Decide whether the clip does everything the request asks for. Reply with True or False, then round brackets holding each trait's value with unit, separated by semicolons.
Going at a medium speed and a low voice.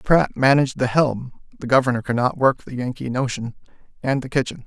True (195 wpm; 130 Hz)